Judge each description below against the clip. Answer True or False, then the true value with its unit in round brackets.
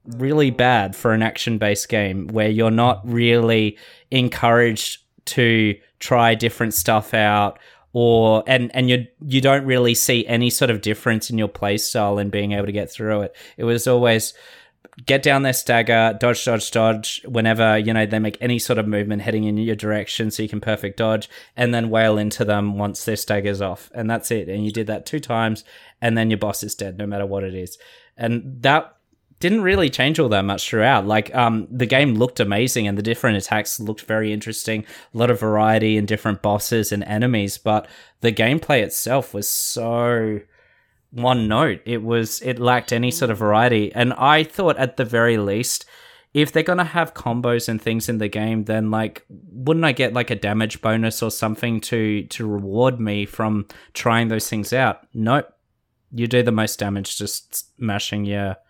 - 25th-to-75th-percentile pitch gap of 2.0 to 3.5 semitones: True (2.4 semitones)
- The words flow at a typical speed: True (195 wpm)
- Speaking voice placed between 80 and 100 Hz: False (110 Hz)